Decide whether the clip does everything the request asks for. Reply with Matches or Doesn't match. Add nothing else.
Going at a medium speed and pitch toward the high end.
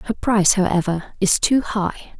Matches